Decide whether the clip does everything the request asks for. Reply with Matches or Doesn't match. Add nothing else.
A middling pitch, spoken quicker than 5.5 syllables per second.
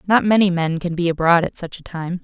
Matches